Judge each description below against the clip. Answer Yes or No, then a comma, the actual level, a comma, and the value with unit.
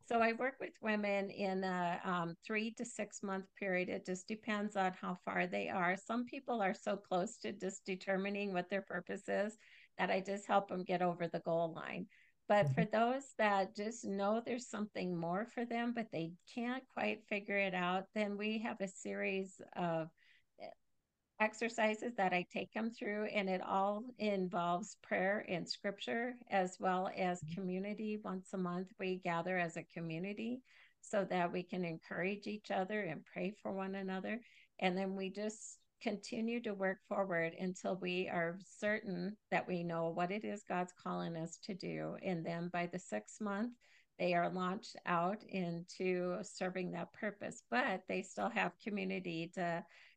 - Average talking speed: Yes, average, 175 wpm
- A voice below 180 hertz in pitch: No, high, 190 Hz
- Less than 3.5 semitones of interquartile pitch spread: Yes, average, 2.9 semitones